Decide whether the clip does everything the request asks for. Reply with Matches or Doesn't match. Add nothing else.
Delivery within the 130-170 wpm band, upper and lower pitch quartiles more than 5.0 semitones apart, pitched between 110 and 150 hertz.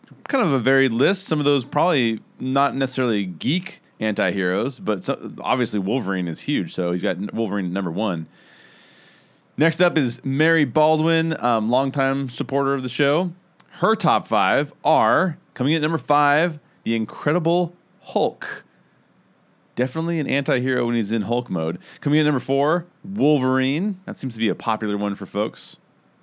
Matches